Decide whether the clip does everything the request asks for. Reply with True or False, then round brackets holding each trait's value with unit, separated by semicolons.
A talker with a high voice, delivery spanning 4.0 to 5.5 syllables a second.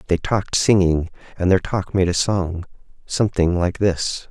False (90 Hz; 4.7 syllables/s)